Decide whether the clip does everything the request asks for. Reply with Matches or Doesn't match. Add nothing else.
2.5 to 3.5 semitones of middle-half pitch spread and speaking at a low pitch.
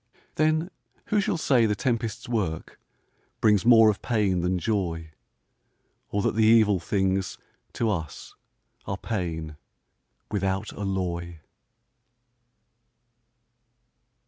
Doesn't match